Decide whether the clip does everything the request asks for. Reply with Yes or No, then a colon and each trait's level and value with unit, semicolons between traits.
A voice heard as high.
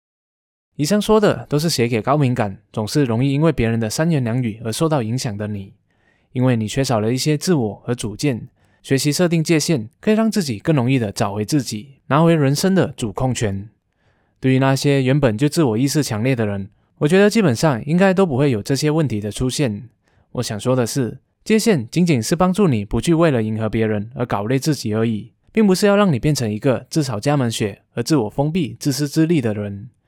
No: low, 130 Hz